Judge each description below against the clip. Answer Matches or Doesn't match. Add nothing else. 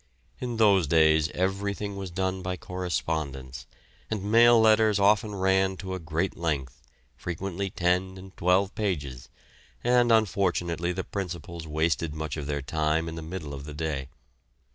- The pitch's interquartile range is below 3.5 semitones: Doesn't match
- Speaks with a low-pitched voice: Matches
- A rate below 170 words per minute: Matches